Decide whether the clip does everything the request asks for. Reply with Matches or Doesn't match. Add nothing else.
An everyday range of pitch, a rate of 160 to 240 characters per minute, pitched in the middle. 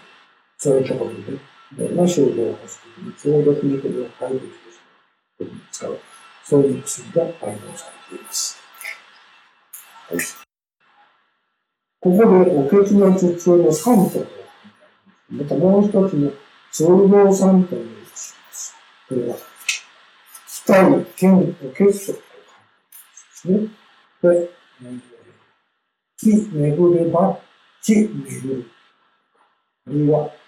Matches